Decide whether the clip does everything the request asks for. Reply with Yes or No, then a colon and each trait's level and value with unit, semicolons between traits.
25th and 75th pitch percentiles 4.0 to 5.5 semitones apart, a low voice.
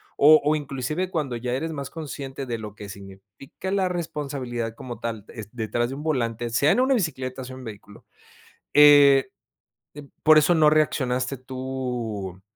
Yes: average, 4.3 semitones; low, 130 Hz